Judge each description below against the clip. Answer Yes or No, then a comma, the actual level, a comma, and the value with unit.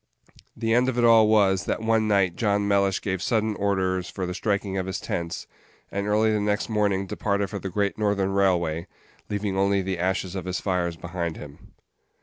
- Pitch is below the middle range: Yes, low, 100 Hz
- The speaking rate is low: No, average, 195 wpm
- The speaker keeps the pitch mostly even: Yes, narrow, 2.2 semitones